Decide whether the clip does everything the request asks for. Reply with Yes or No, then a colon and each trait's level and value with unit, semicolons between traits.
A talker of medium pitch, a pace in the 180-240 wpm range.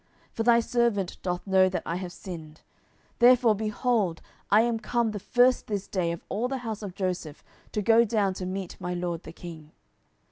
No: high, 200 Hz; average, 200 wpm